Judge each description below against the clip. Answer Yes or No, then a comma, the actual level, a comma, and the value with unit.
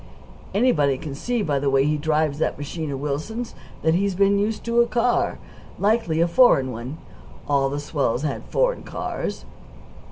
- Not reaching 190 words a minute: Yes, average, 170 wpm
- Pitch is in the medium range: Yes, medium, 155 Hz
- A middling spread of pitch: No, wide, 7.2 semitones